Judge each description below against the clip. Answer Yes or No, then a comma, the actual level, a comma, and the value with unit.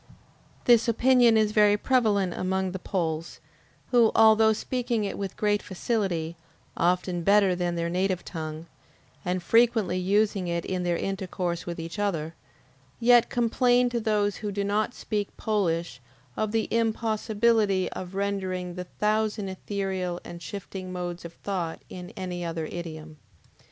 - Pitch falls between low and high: No, high, 195 Hz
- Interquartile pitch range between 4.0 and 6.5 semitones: No, average, 3.5 semitones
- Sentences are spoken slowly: No, average, 145 wpm